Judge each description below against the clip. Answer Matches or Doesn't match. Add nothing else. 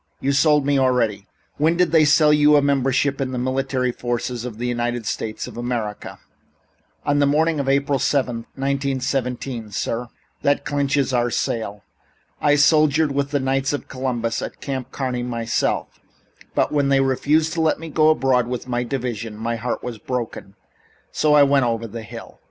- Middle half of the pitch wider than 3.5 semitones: Doesn't match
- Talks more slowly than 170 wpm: Doesn't match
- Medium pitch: Doesn't match